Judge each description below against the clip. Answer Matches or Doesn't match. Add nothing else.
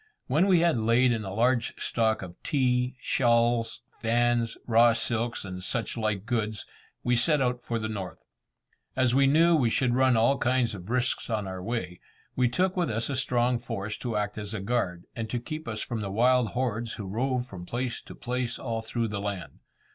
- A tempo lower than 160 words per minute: Doesn't match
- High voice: Doesn't match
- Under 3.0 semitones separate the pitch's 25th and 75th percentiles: Matches